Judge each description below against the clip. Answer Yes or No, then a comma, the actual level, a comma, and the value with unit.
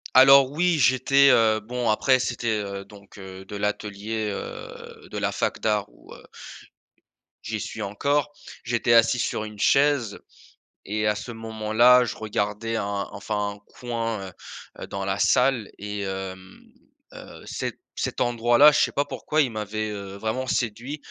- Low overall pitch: Yes, low, 110 Hz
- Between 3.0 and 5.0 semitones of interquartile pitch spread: Yes, average, 3.3 semitones